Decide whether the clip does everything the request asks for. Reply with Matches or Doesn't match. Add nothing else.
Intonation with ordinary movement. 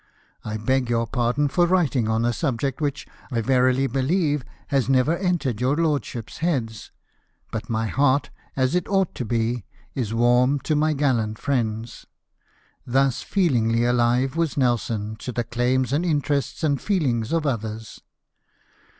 Matches